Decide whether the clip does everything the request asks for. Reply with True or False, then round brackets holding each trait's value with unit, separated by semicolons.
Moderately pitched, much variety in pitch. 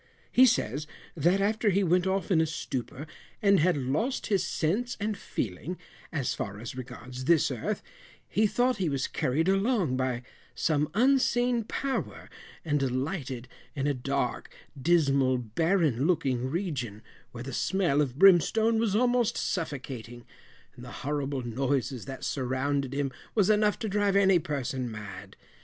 True (150 Hz; 7.3 semitones)